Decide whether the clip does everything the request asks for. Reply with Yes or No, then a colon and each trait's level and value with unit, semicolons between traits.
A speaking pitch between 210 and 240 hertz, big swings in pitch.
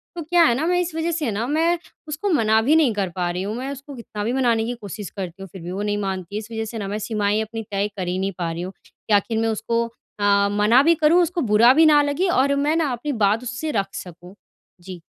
Yes: high, 225 Hz; wide, 6.5 semitones